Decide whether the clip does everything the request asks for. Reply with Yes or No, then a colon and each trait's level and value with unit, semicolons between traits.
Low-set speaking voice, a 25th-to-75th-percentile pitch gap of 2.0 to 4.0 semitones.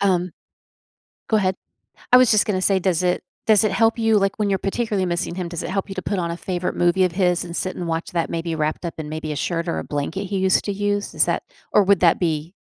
No: medium, 185 Hz; average, 2.9 semitones